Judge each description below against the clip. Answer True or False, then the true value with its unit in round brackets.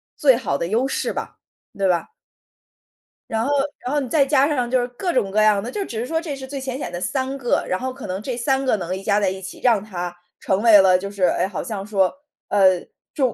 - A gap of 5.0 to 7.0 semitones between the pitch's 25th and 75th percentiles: True (5.5 semitones)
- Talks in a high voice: True (225 Hz)